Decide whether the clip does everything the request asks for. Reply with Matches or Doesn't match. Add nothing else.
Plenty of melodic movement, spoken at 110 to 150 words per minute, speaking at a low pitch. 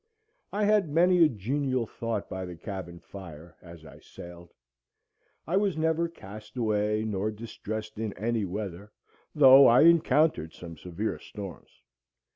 Matches